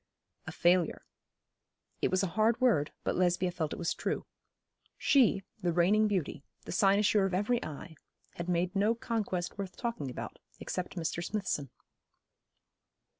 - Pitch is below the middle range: No, medium, 185 Hz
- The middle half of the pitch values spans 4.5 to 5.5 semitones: No, average, 3.4 semitones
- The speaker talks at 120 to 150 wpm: Yes, average, 145 wpm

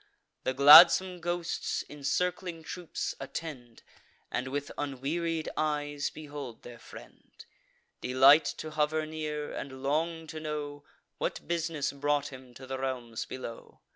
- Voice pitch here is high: No, medium, 145 Hz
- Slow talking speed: Yes, slow, 130 wpm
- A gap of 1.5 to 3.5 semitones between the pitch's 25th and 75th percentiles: Yes, average, 2.9 semitones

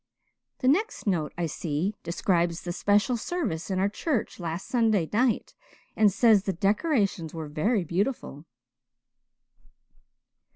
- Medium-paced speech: No, slow, 125 wpm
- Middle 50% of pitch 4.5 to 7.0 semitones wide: Yes, average, 5.2 semitones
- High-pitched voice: Yes, high, 195 Hz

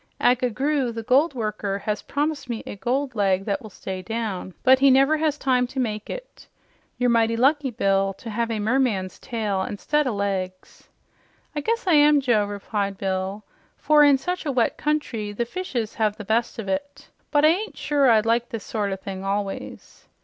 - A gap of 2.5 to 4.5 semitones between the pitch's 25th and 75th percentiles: No, average, 5.3 semitones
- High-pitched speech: Yes, high, 230 Hz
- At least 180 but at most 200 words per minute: Yes, average, 195 wpm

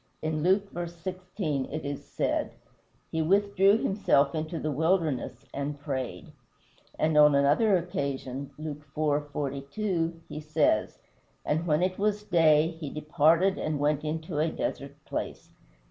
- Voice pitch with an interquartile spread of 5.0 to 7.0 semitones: No, average, 3.4 semitones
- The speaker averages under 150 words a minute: Yes, average, 140 wpm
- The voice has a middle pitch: Yes, medium, 155 Hz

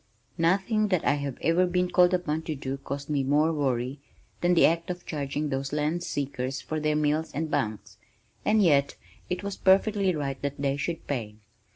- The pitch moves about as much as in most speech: Yes, average, 4.1 semitones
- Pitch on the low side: No, medium, 150 Hz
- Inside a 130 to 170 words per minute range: No, average, 190 wpm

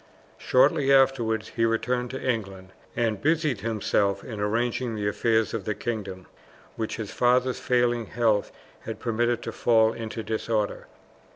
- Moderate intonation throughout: No, narrow, 2.2 semitones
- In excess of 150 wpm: No, average, 145 wpm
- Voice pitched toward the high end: No, low, 115 Hz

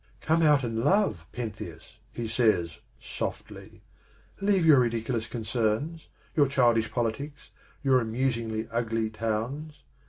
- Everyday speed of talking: No, slow, 120 wpm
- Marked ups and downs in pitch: No, average, 4.1 semitones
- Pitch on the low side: Yes, low, 120 Hz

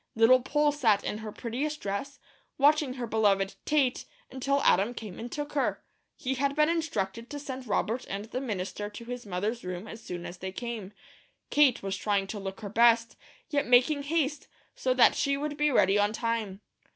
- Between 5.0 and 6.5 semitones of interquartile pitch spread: Yes, wide, 5.4 semitones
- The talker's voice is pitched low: No, high, 235 Hz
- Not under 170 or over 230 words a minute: Yes, average, 190 wpm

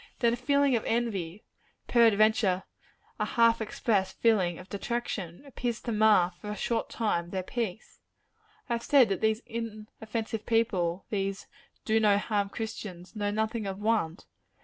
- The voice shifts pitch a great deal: No, average, 2.9 semitones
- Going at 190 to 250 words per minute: No, average, 150 wpm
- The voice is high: Yes, high, 215 Hz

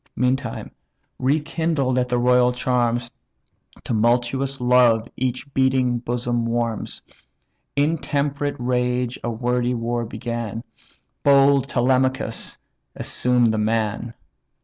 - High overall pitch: No, low, 125 Hz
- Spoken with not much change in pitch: Yes, narrow, 1.8 semitones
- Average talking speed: No, slow, 100 wpm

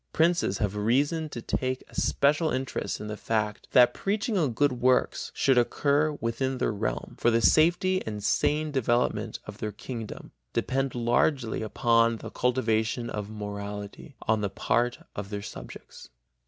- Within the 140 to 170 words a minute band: Yes, average, 155 wpm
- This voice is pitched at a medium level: No, low, 120 Hz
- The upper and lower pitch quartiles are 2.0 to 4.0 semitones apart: No, average, 4.6 semitones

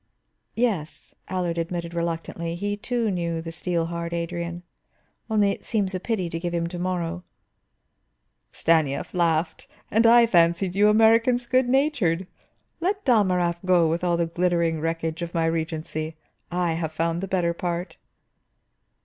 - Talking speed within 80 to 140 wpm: No, average, 150 wpm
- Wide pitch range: No, average, 3.0 semitones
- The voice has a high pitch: No, medium, 175 Hz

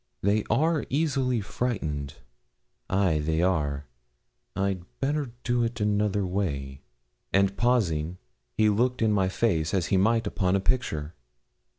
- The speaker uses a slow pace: Yes, slow, 130 wpm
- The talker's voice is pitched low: Yes, low, 100 Hz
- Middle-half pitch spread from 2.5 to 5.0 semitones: No, wide, 5.6 semitones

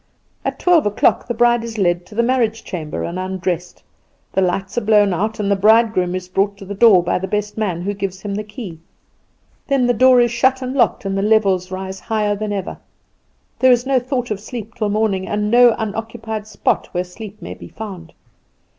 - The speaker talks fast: Yes, fast, 210 wpm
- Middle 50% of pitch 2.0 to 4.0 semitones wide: Yes, average, 3.4 semitones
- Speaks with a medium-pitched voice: No, high, 210 Hz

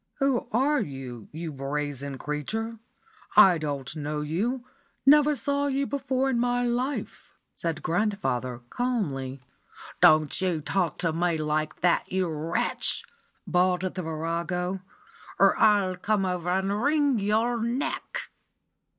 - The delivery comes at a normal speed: No, slow, 125 wpm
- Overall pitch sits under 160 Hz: No, medium, 185 Hz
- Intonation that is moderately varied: No, wide, 7.7 semitones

